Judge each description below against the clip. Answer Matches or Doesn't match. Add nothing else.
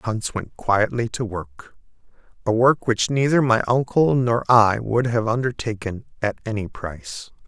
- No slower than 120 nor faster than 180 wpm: Matches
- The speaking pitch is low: Matches